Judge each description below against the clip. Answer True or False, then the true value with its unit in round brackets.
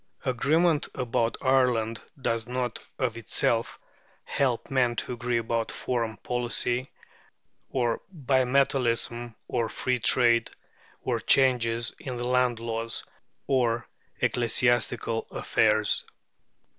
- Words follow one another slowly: True (95 wpm)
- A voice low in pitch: True (120 Hz)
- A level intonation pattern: True (1.7 semitones)